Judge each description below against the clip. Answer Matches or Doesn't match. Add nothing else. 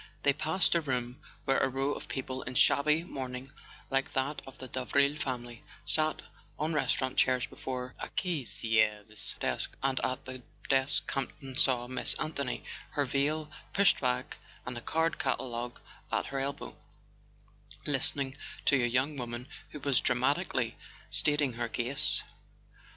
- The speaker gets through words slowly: Doesn't match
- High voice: Doesn't match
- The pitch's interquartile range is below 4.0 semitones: Matches